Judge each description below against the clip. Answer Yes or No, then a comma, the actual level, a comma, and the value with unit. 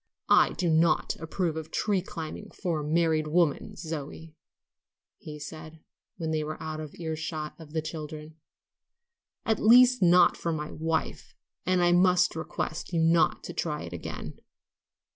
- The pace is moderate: Yes, average, 160 wpm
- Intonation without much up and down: Yes, narrow, 2.1 semitones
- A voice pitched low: No, medium, 160 Hz